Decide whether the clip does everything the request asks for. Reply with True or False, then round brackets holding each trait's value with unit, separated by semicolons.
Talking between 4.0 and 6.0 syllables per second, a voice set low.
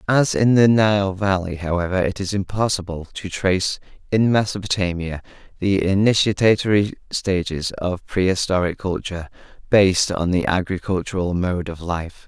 True (5.1 syllables/s; 95 Hz)